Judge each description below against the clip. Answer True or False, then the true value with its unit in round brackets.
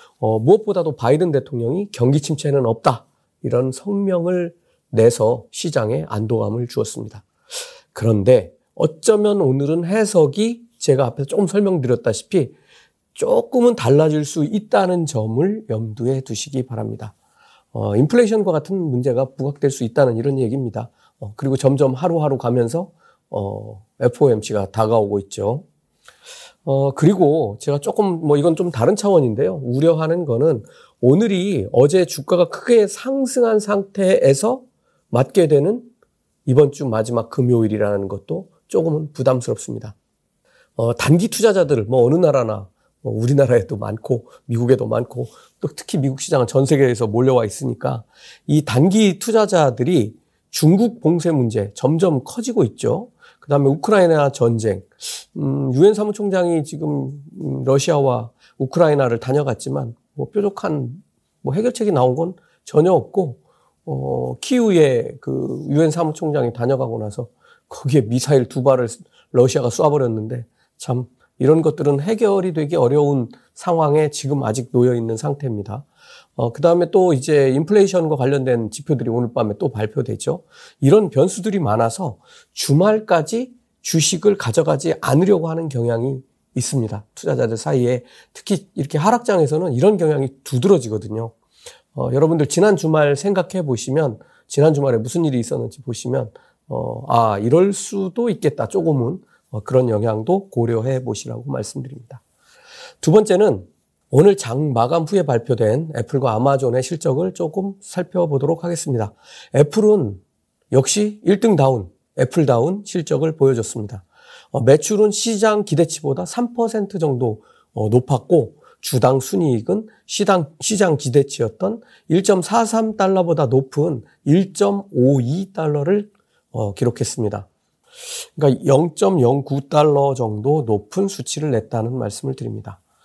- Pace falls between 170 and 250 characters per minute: False (305 characters per minute)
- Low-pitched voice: False (145 Hz)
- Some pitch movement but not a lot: False (6.8 semitones)